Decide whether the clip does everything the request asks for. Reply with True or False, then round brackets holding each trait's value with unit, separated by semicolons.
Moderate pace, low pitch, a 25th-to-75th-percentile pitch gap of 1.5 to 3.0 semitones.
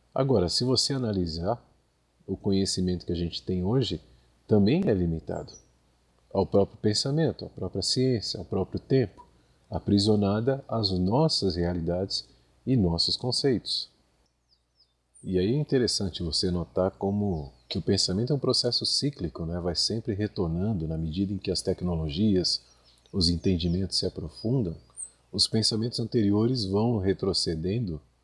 False (135 wpm; 95 Hz; 4.9 semitones)